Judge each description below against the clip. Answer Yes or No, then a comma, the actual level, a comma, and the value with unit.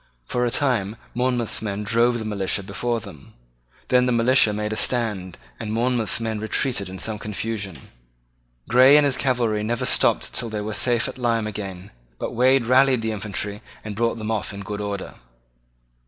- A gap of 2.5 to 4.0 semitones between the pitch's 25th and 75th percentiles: Yes, average, 2.9 semitones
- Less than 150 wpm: No, average, 180 wpm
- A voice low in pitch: Yes, low, 110 Hz